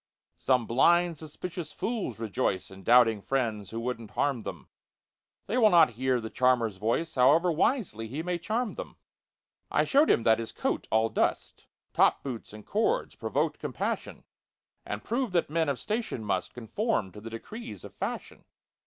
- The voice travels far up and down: Yes, wide, 7.8 semitones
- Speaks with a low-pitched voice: Yes, low, 130 Hz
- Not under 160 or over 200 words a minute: Yes, average, 165 wpm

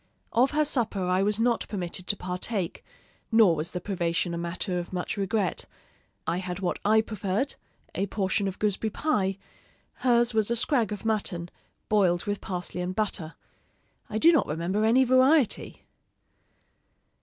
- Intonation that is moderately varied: Yes, average, 3.8 semitones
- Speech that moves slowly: No, average, 155 wpm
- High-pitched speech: Yes, high, 200 Hz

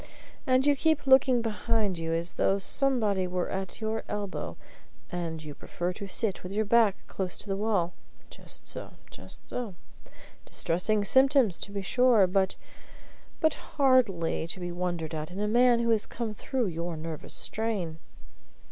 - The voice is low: No, high, 200 Hz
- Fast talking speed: No, average, 165 wpm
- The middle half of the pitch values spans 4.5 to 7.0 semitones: Yes, average, 4.9 semitones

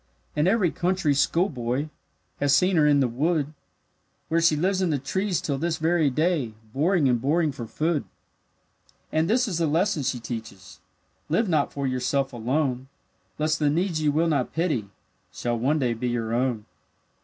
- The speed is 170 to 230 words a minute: Yes, average, 175 wpm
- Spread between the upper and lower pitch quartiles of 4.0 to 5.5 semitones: Yes, average, 4.8 semitones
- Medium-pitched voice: Yes, medium, 150 Hz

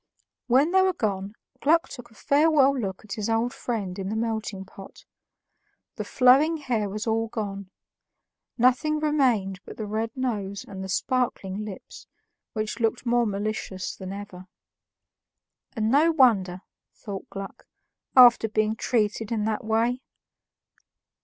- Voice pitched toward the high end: Yes, high, 220 Hz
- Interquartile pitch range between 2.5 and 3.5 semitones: No, average, 4.0 semitones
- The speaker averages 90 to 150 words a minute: Yes, average, 140 wpm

